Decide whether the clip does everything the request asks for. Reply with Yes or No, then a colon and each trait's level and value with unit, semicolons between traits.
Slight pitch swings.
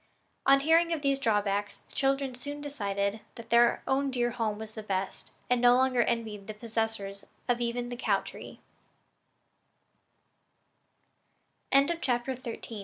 No: average, 4.2 semitones